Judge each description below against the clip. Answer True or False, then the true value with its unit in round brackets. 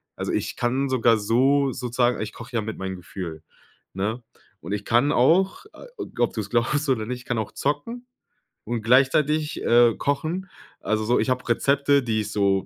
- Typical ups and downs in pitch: True (4.3 semitones)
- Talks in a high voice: False (120 Hz)